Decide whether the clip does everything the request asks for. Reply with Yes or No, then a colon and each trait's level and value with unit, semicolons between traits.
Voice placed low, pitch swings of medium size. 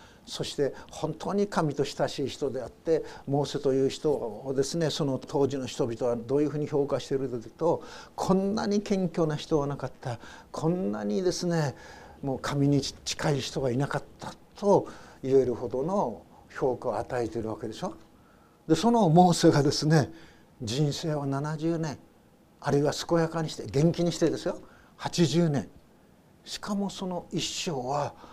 No: medium, 145 Hz; average, 3.8 semitones